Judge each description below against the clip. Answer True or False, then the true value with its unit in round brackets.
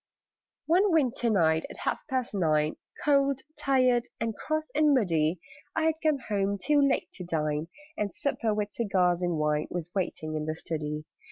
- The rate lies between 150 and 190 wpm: True (170 wpm)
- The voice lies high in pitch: True (200 Hz)